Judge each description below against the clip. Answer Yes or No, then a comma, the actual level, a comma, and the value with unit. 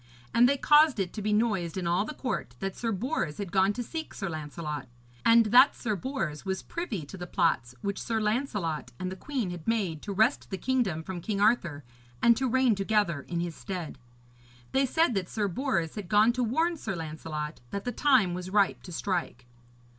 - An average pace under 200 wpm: No, fast, 205 wpm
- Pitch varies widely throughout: Yes, wide, 5.7 semitones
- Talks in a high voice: Yes, high, 200 Hz